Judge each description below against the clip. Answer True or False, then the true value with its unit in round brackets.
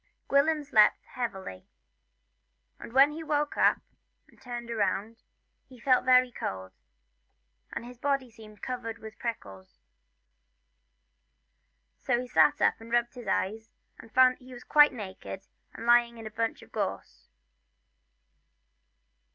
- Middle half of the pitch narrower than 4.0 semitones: True (2.8 semitones)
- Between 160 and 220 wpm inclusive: False (135 wpm)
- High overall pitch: True (235 Hz)